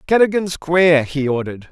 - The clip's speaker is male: Yes, male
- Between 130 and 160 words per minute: Yes, average, 140 wpm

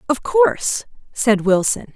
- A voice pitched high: Yes, high, 245 Hz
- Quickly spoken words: No, slow, 125 wpm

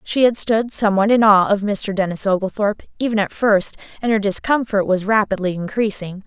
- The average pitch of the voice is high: Yes, high, 205 Hz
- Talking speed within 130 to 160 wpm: No, average, 180 wpm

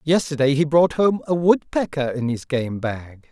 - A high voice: No, medium, 145 Hz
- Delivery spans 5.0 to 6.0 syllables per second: No, 4.5 syllables/s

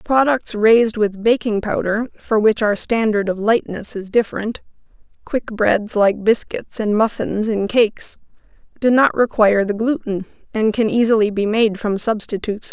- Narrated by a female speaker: Yes, female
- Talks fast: No, average, 150 wpm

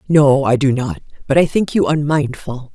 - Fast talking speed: No, average, 195 wpm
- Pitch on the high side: No, medium, 145 Hz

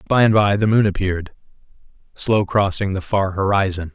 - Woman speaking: No, male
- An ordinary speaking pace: Yes, average, 165 wpm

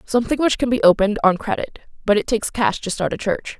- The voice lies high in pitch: Yes, high, 215 Hz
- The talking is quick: Yes, fast, 250 wpm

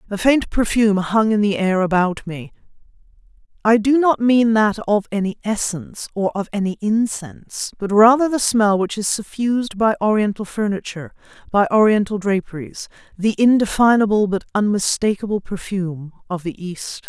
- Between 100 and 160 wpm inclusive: Yes, average, 150 wpm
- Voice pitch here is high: Yes, high, 210 Hz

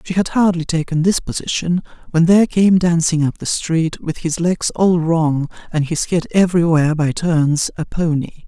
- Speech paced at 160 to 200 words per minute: Yes, average, 185 wpm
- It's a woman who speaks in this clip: No, male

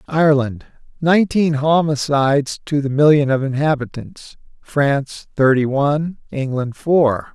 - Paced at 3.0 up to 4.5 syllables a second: Yes, 4.4 syllables/s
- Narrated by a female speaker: No, male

